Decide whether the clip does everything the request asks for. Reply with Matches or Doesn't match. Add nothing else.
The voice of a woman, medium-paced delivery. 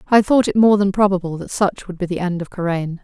Doesn't match